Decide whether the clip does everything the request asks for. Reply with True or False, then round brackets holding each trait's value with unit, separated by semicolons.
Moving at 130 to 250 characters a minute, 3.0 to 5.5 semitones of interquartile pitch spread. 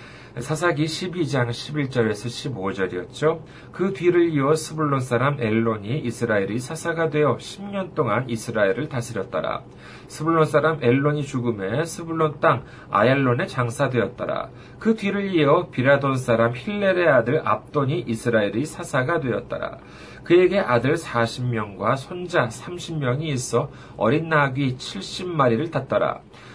False (280 characters per minute; 5.1 semitones)